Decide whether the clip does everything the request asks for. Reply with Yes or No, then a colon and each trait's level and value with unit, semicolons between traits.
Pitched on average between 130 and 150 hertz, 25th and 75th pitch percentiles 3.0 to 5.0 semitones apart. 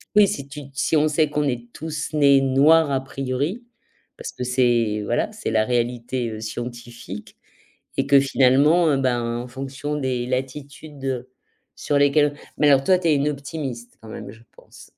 Yes: low, 135 Hz; average, 3.3 semitones